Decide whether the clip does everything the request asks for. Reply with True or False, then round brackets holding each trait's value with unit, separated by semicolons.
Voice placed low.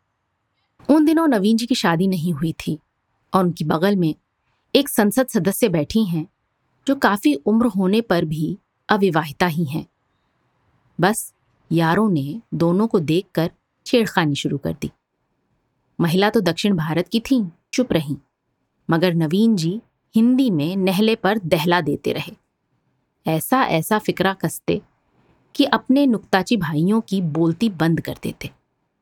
False (185 Hz)